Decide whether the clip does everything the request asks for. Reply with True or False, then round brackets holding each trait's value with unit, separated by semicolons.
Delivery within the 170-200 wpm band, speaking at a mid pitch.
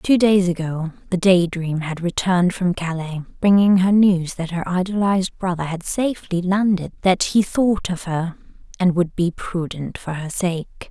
True (175 wpm; 180 Hz)